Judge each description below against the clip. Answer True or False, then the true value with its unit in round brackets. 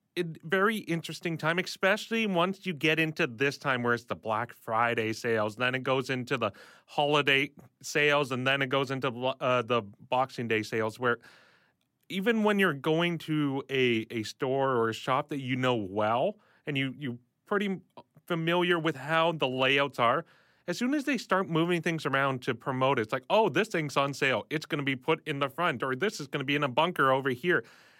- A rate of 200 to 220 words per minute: True (205 wpm)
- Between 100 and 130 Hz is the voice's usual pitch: False (140 Hz)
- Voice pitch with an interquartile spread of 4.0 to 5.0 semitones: True (4.5 semitones)